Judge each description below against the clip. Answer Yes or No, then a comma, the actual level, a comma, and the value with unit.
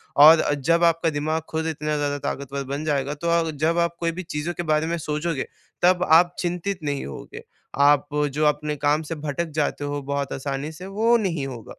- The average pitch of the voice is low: No, medium, 155 Hz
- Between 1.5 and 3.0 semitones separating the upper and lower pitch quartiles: Yes, average, 2.7 semitones